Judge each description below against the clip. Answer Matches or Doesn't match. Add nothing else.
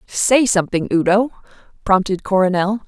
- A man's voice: Doesn't match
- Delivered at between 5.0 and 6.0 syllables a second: Matches